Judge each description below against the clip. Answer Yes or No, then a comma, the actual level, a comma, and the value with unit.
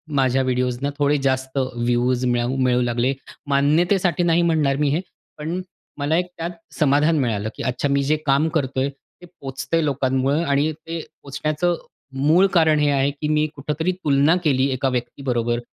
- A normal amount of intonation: Yes, average, 3.1 semitones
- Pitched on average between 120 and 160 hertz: Yes, medium, 140 Hz